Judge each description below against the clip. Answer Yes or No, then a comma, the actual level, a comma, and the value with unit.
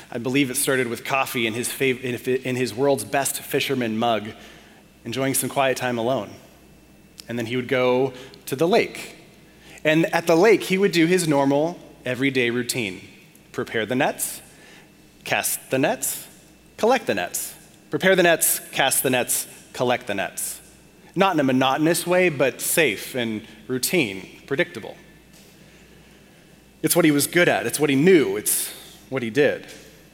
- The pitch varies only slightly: No, average, 5.0 semitones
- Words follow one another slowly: No, average, 160 wpm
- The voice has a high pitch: No, low, 135 Hz